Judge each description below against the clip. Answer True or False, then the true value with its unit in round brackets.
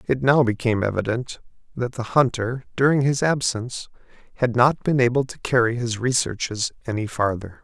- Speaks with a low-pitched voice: True (120 Hz)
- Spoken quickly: False (155 wpm)